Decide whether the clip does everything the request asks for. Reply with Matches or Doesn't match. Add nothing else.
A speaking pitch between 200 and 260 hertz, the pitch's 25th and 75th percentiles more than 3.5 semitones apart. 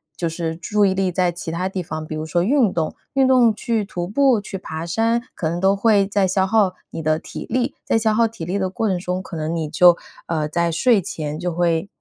Doesn't match